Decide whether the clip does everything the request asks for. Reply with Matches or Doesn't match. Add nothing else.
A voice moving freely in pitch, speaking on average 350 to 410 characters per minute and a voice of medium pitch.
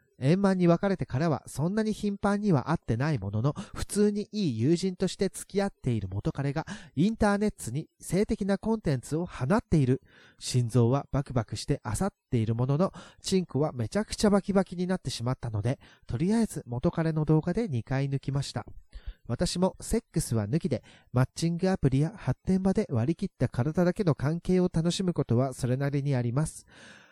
Matches